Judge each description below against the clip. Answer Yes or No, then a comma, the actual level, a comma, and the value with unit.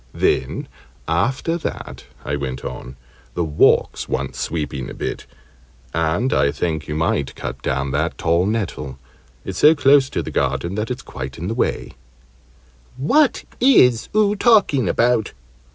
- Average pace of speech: Yes, average, 150 wpm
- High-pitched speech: No, very low, 85 Hz